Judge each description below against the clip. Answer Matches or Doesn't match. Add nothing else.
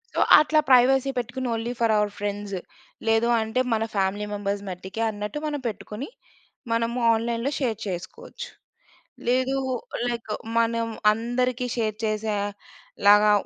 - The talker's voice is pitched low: Doesn't match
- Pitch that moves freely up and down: Doesn't match